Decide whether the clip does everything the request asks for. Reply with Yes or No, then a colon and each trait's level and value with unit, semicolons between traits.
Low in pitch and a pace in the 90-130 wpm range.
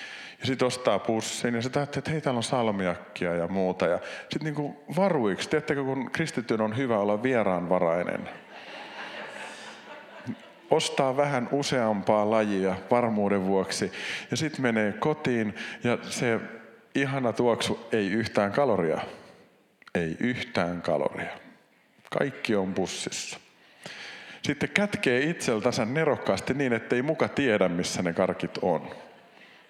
Yes: low, 120 Hz; average, 125 wpm